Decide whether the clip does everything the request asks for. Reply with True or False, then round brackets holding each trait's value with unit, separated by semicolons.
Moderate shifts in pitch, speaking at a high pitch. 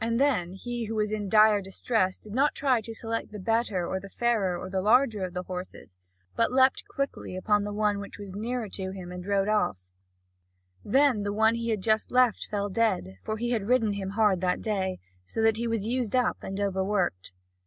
True (3.2 semitones; 210 Hz)